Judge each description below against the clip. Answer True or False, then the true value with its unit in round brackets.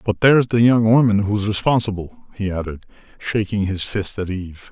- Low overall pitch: True (105 Hz)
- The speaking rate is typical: True (180 wpm)